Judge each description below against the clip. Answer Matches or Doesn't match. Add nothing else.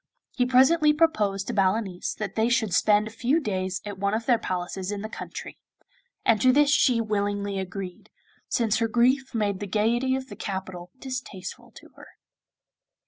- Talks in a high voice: Matches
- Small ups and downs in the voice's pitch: Doesn't match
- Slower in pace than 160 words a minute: Doesn't match